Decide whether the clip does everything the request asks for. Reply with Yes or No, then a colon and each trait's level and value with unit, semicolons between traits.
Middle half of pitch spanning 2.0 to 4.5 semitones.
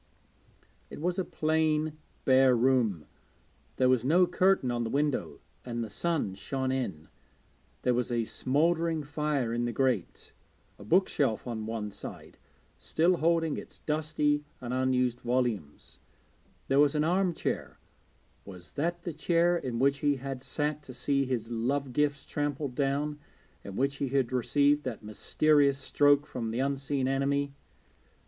Yes: average, 3.5 semitones